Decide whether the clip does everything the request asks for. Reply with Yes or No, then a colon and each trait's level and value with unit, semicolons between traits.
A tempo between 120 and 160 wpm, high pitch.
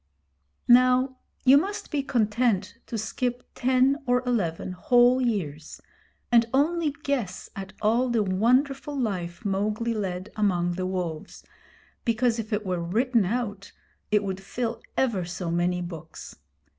Yes: slow, 135 wpm; high, 220 Hz